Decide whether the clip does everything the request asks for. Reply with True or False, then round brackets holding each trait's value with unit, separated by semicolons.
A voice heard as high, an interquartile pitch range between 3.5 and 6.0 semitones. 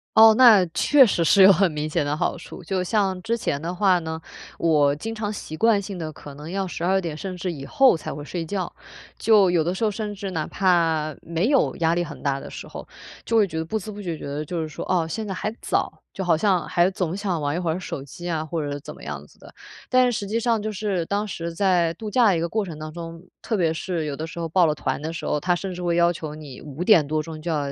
False (175 Hz; 4.1 semitones)